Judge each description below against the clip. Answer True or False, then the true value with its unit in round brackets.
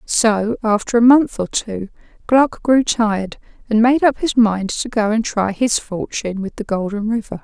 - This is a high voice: True (220 Hz)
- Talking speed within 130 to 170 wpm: False (195 wpm)